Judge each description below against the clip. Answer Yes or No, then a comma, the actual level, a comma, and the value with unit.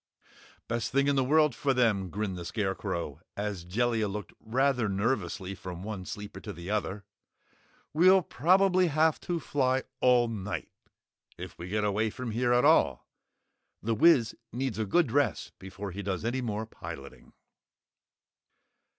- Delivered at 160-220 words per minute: No, average, 150 wpm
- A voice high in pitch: No, low, 110 Hz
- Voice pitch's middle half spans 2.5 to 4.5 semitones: No, average, 5.1 semitones